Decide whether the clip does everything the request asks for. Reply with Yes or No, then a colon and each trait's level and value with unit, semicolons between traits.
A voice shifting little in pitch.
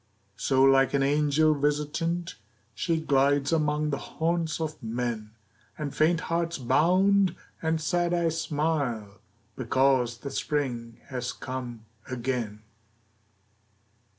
No: average, 4.2 semitones